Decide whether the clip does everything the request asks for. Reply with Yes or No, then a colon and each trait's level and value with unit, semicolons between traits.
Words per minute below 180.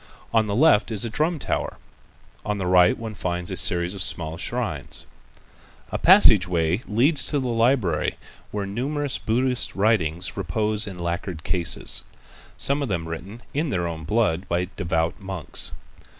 Yes: average, 160 wpm